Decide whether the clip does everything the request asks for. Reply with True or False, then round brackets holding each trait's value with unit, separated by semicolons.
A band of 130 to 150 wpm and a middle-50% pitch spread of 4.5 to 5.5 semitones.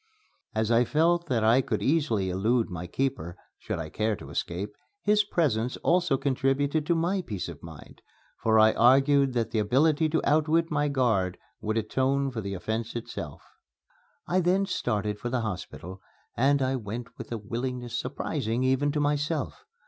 False (170 wpm; 5.1 semitones)